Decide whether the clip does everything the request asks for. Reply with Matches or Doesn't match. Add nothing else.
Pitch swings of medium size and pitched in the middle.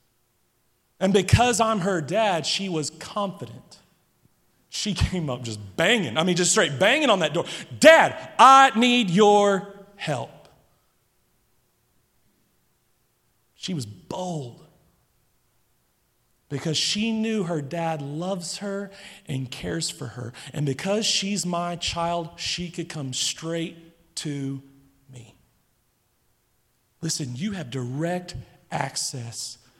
Doesn't match